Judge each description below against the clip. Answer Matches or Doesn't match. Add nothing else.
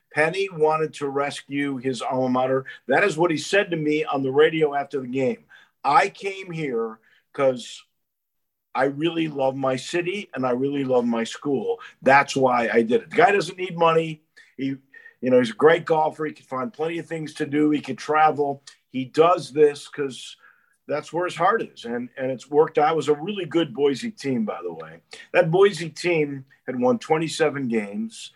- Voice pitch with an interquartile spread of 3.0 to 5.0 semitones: Matches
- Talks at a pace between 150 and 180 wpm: Doesn't match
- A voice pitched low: Doesn't match